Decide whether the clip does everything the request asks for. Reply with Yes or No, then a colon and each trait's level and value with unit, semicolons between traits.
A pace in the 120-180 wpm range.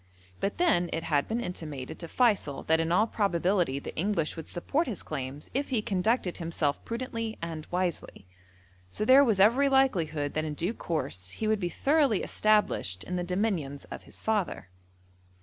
Yes: average, 175 wpm